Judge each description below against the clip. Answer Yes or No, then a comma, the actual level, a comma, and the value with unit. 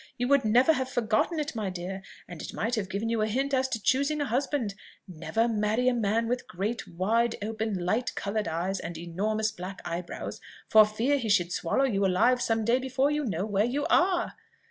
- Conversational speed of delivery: No, fast, 210 wpm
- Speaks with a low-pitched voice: No, high, 220 Hz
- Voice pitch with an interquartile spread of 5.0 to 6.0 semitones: No, average, 4.5 semitones